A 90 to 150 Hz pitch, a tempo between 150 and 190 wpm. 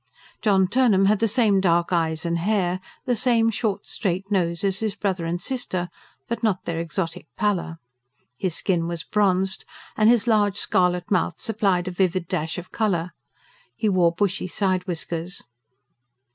No: high, 190 Hz; average, 160 wpm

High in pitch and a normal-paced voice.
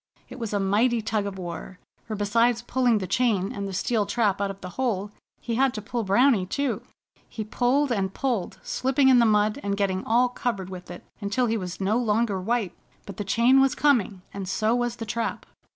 No: high, 215 Hz; fast, 210 wpm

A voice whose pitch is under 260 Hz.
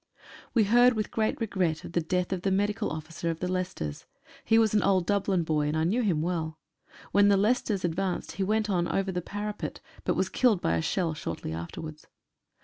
Yes: medium, 185 Hz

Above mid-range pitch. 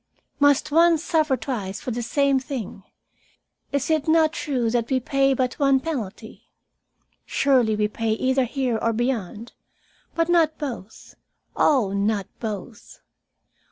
Yes: very high, 260 Hz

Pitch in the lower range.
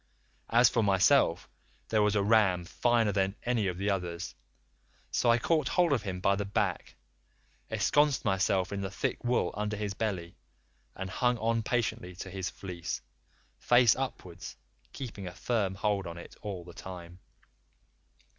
Yes: low, 100 Hz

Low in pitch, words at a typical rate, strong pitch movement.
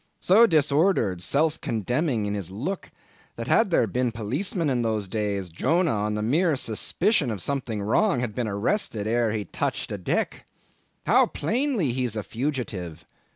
Yes: low, 120 Hz; average, 160 wpm; wide, 6.8 semitones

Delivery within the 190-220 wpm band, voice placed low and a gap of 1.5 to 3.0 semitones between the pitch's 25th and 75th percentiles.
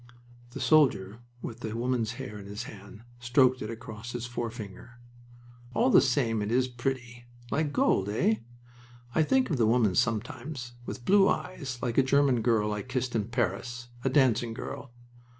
No: average, 170 wpm; low, 120 Hz; average, 2.7 semitones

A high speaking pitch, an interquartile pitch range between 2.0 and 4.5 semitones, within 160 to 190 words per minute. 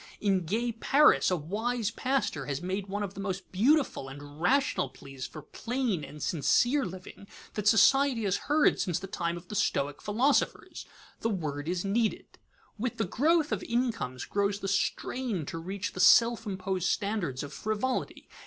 No: high, 200 Hz; wide, 5.4 semitones; average, 170 wpm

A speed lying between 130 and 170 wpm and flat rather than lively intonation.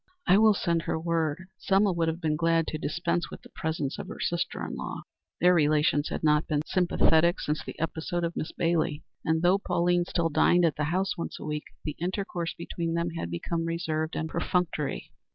No: fast, 205 wpm; narrow, 1.8 semitones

